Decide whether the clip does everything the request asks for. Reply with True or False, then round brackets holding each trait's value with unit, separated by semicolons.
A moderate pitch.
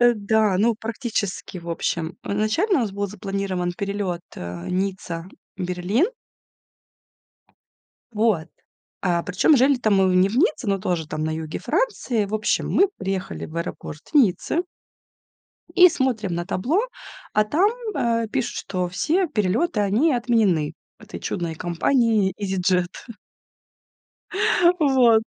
False (200 Hz)